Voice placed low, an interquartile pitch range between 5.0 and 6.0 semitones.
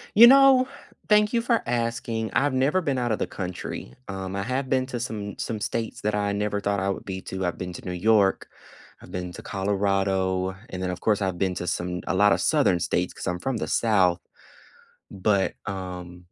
No: low, 100 Hz; average, 4.1 semitones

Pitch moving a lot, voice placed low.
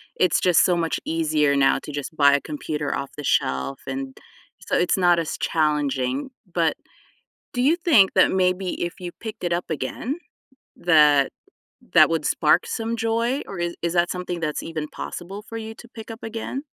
No: wide, 6.5 semitones; medium, 175 Hz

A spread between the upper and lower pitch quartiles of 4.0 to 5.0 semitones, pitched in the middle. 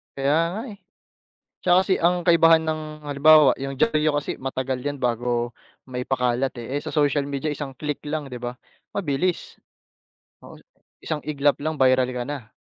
No: average, 3.1 semitones; medium, 145 Hz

